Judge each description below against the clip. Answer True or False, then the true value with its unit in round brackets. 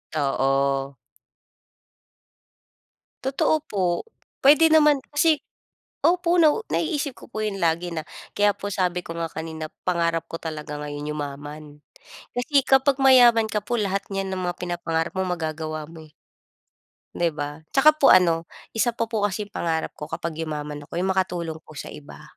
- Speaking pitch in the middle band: True (175 Hz)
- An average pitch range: False (6.6 semitones)